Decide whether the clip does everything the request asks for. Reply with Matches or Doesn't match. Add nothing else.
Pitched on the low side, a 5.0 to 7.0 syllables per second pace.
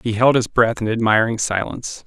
Matches